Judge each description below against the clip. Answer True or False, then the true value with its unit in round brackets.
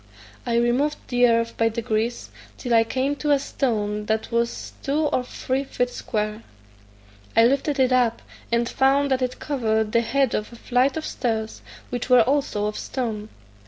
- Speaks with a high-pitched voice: True (240 Hz)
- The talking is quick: False (175 wpm)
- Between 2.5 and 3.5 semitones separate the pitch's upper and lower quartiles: True (2.9 semitones)